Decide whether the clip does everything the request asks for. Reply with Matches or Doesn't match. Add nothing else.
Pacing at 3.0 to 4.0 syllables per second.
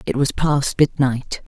Matches